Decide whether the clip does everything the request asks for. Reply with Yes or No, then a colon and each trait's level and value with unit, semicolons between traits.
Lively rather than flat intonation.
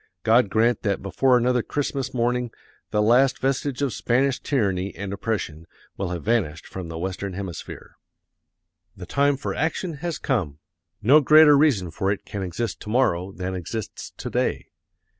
Yes: wide, 6.0 semitones